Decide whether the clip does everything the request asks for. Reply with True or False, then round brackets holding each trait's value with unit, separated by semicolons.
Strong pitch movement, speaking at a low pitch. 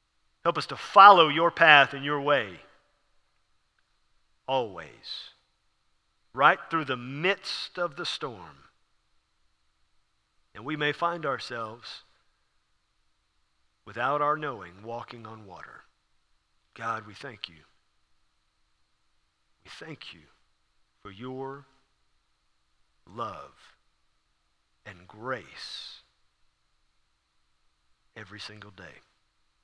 True (8.9 semitones; 120 Hz)